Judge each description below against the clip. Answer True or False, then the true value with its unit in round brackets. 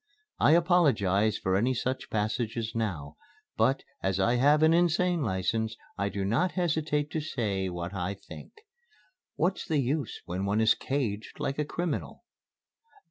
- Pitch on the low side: True (115 Hz)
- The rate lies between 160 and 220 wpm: False (150 wpm)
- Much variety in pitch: True (7.3 semitones)